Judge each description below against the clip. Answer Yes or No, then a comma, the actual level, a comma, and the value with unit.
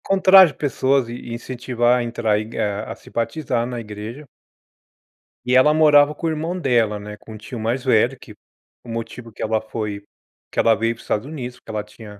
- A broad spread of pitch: No, average, 3.6 semitones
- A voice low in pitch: Yes, low, 120 Hz